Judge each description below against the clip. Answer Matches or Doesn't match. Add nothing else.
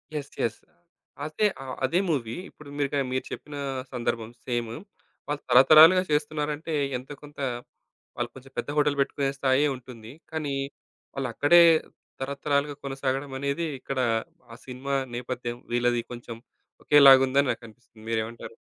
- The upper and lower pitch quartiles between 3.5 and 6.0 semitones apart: Doesn't match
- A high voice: Doesn't match